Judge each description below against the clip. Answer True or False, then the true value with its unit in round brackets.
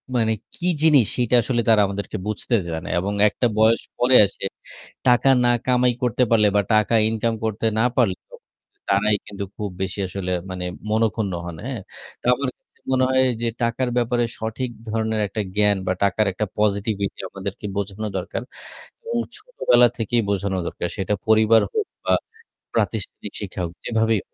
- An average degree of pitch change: True (3.2 semitones)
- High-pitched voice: False (110 Hz)